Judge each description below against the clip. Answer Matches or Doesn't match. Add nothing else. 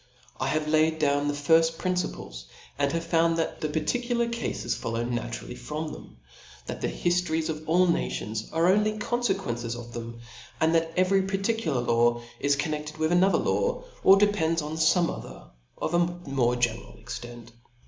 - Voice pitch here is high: Doesn't match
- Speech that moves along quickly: Doesn't match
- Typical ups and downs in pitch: Doesn't match